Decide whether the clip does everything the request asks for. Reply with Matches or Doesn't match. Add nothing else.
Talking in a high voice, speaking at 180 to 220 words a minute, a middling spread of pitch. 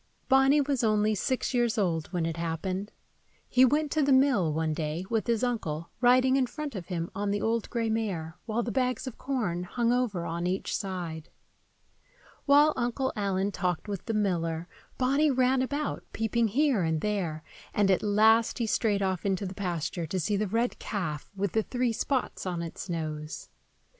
Doesn't match